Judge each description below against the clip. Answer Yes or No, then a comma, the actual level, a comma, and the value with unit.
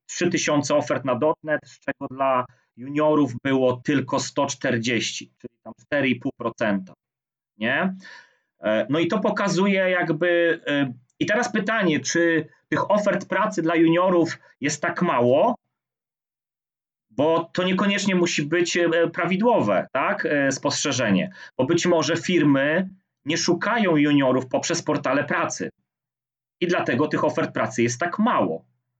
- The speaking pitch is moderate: Yes, medium, 155 Hz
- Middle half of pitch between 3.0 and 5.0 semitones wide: Yes, average, 4.4 semitones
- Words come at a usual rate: Yes, average, 120 wpm